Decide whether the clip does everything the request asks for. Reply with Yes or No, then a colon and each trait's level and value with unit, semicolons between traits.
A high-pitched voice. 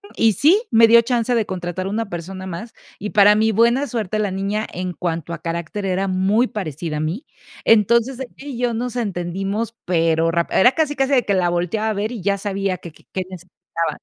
Yes: high, 200 Hz